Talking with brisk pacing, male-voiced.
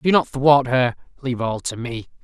Yes: fast, 215 wpm; male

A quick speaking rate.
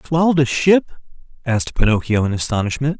No: average, 140 wpm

